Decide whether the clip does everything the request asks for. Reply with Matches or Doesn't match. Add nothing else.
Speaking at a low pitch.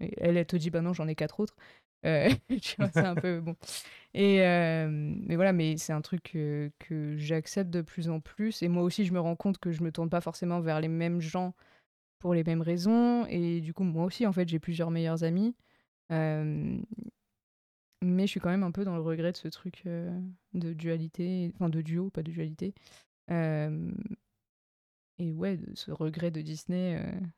Doesn't match